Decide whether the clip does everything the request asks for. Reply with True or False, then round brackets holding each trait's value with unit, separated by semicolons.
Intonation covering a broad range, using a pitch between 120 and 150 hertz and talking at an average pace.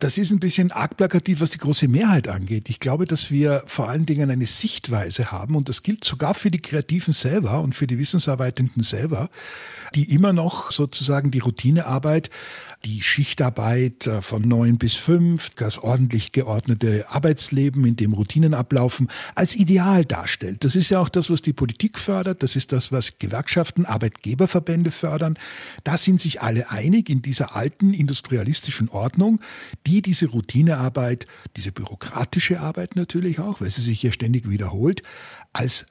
True (6.0 semitones; 140 Hz; 160 wpm)